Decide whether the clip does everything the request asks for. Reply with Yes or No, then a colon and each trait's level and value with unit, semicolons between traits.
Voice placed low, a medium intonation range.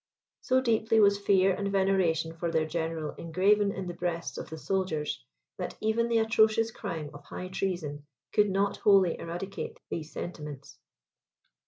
No: medium, 185 Hz; average, 3.9 semitones